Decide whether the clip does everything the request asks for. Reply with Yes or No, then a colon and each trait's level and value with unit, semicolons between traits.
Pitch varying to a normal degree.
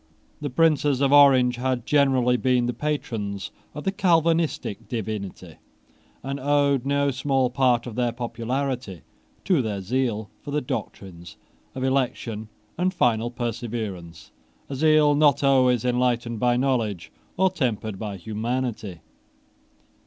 Yes: average, 3.9 semitones